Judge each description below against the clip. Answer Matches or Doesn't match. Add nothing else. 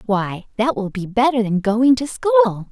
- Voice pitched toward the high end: Matches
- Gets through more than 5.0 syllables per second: Doesn't match